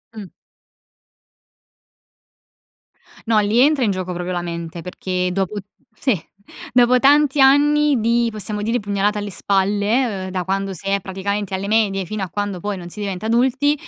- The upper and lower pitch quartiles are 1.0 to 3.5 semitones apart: No, average, 3.9 semitones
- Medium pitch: No, high, 205 Hz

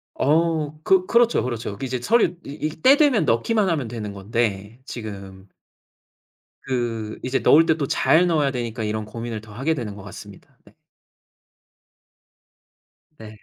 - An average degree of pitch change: No, wide, 6.8 semitones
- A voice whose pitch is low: Yes, low, 120 Hz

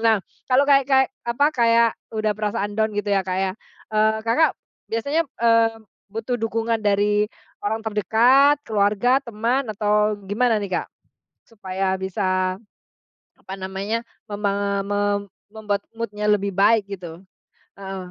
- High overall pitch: Yes, high, 210 Hz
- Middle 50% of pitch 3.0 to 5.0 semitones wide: No, narrow, 2.4 semitones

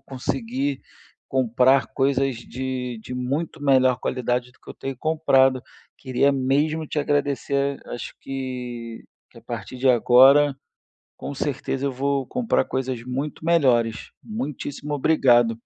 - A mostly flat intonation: Yes, narrow, 2.0 semitones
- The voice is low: Yes, low, 130 Hz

